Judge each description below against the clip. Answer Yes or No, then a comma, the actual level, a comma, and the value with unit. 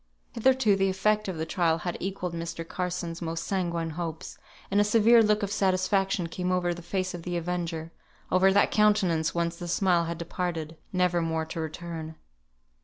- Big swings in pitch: No, narrow, 2.5 semitones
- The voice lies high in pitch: No, medium, 175 Hz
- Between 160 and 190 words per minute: Yes, average, 180 wpm